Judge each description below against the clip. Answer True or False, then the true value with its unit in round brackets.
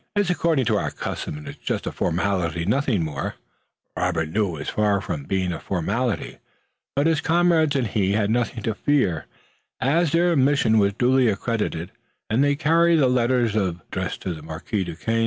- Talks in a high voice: False (110 Hz)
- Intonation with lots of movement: True (7.6 semitones)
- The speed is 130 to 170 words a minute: False (180 wpm)